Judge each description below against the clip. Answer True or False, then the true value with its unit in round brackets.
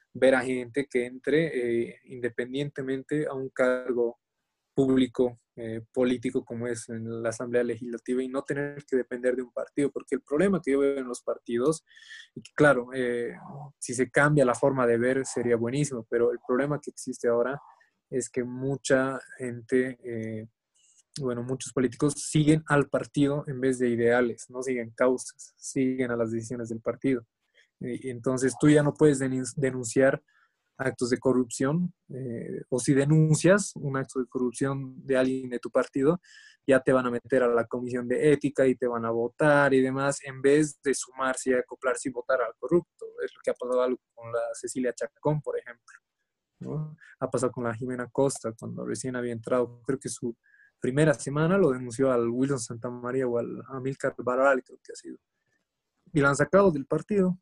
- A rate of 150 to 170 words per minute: False (180 wpm)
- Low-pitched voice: True (130 Hz)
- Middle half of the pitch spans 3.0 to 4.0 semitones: False (2.4 semitones)